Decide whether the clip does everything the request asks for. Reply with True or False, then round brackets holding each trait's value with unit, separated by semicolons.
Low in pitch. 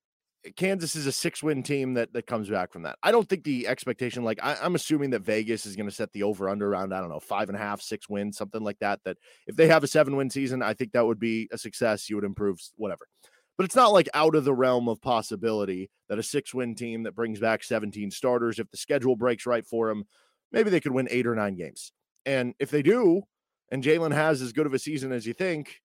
True (120 Hz)